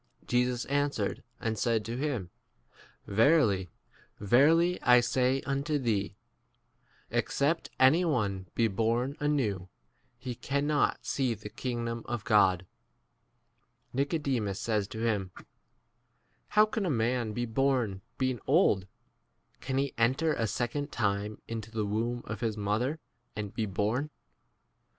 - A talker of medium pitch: No, low, 120 Hz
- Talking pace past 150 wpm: No, slow, 135 wpm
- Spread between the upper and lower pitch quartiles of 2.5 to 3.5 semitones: No, average, 4.5 semitones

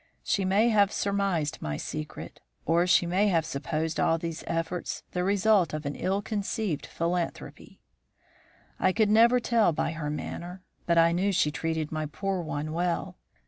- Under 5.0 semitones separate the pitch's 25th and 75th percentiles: Yes, average, 3.7 semitones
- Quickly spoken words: No, average, 165 wpm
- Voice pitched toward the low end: No, medium, 175 Hz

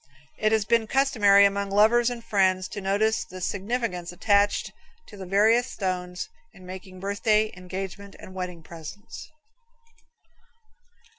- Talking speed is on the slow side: Yes, slow, 130 wpm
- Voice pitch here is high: Yes, high, 200 Hz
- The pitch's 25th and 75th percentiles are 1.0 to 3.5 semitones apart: Yes, average, 2.7 semitones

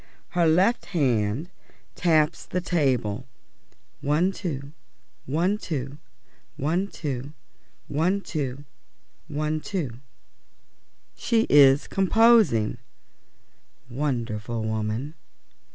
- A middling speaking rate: No, slow, 80 wpm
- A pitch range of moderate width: No, wide, 5.8 semitones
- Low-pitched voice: No, medium, 150 Hz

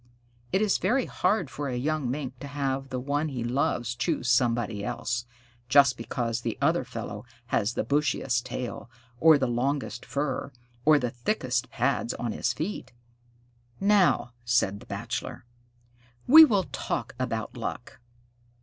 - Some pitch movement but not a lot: Yes, average, 3.8 semitones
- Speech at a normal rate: Yes, average, 150 wpm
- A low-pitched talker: Yes, low, 130 Hz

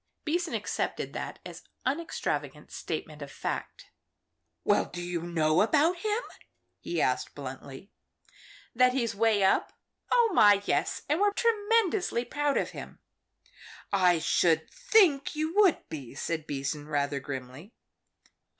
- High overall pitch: Yes, high, 200 Hz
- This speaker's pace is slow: Yes, slow, 130 wpm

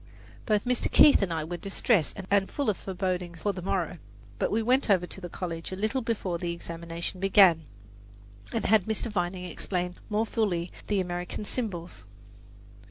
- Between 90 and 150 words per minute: No, average, 170 wpm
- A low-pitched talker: No, medium, 185 Hz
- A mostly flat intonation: No, average, 3.4 semitones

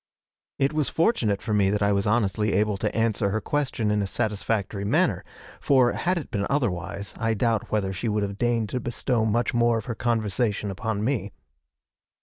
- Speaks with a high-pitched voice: No, low, 110 Hz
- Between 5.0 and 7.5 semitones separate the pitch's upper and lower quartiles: No, average, 2.9 semitones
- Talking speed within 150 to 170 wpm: No, average, 190 wpm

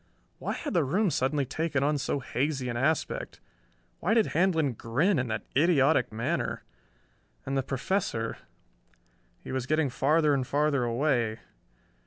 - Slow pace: No, average, 145 wpm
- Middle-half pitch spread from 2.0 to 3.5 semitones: No, average, 4.0 semitones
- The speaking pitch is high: No, medium, 140 Hz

